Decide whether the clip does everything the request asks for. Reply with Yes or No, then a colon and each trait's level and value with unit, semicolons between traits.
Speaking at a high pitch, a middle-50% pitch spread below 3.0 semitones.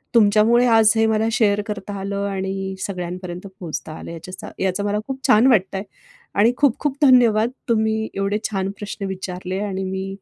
Yes: high, 200 Hz; narrow, 2.4 semitones